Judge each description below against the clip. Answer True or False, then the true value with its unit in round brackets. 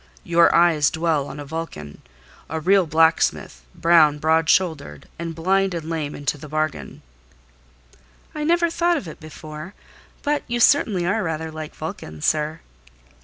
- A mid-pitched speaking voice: True (160 Hz)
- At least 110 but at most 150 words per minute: True (145 wpm)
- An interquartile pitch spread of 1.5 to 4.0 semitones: True (2.7 semitones)